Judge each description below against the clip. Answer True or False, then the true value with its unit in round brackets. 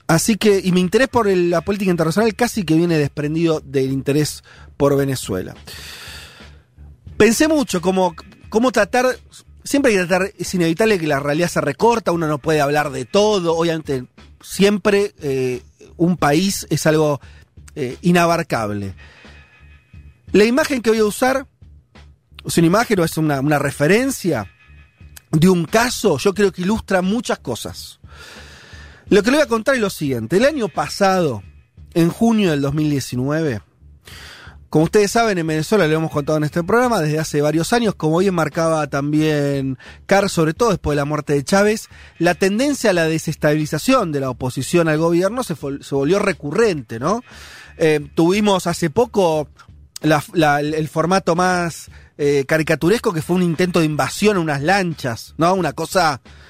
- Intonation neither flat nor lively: False (5.7 semitones)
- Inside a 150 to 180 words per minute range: True (165 wpm)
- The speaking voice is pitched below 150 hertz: False (165 Hz)